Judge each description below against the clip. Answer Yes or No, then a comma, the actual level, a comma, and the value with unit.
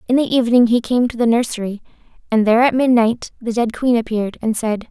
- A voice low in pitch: No, high, 235 Hz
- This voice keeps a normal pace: No, fast, 220 wpm